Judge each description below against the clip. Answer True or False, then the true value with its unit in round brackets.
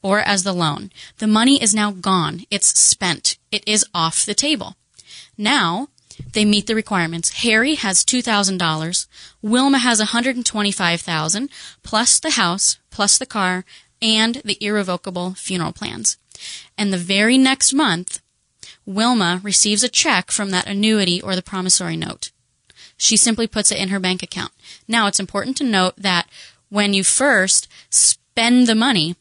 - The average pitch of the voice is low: False (205 Hz)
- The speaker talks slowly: False (150 wpm)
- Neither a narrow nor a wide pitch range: True (3.7 semitones)